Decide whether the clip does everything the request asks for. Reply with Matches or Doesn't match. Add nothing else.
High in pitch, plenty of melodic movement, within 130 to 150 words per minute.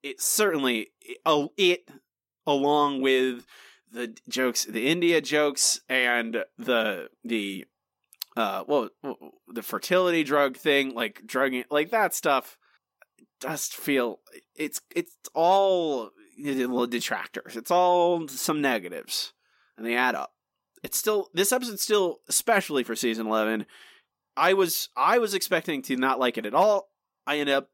Doesn't match